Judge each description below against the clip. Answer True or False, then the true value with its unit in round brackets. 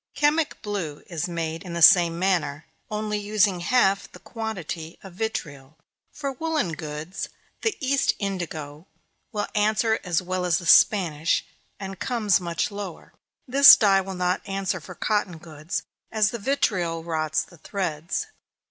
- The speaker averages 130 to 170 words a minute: True (150 wpm)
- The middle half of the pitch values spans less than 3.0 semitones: False (4.2 semitones)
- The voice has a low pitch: False (185 Hz)